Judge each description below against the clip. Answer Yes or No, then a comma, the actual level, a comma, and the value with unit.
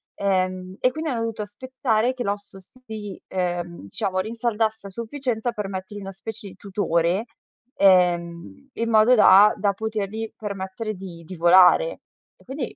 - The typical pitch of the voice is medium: No, high, 205 Hz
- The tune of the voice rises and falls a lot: No, average, 3.3 semitones